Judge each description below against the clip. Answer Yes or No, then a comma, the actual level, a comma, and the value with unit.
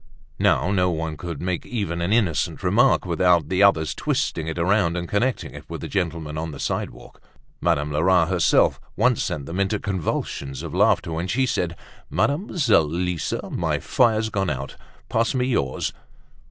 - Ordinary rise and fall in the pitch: Yes, average, 4.2 semitones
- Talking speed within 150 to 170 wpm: Yes, average, 165 wpm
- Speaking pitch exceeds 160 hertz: No, very low, 90 Hz